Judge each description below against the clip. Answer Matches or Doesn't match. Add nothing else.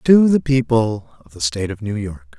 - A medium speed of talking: Doesn't match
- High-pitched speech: Doesn't match